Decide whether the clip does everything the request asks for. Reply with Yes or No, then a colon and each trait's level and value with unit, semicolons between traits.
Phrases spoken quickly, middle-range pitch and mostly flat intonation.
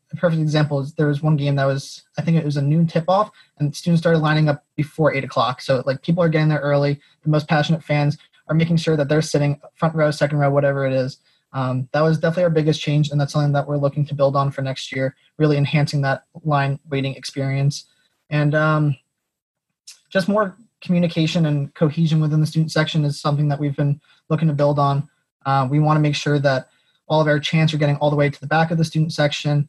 Yes: fast, 240 wpm; medium, 150 Hz; narrow, 1.8 semitones